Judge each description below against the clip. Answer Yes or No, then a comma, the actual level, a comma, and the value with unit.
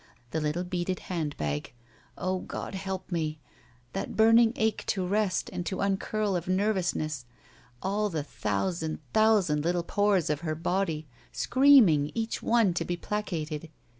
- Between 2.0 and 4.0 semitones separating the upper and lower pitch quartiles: No, average, 4.7 semitones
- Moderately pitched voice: Yes, medium, 180 Hz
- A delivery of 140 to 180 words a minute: Yes, average, 145 wpm